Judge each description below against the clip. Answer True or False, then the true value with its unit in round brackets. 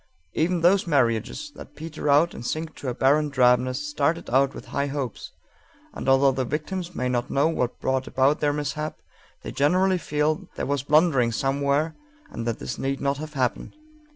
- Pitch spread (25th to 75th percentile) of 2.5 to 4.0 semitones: True (2.9 semitones)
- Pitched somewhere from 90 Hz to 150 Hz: True (140 Hz)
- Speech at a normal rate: True (180 wpm)